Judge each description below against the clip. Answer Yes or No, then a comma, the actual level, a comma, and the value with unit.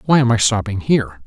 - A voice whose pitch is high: No, low, 115 Hz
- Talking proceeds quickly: Yes, fast, 240 wpm